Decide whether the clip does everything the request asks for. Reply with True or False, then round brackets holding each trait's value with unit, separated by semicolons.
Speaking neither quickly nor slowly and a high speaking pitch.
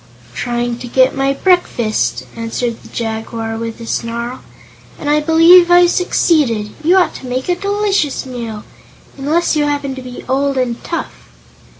True (160 wpm; 265 Hz)